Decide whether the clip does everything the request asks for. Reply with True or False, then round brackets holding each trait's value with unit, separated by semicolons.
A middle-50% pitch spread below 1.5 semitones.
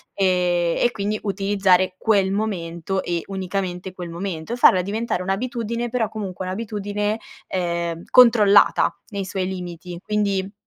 False (2.6 semitones)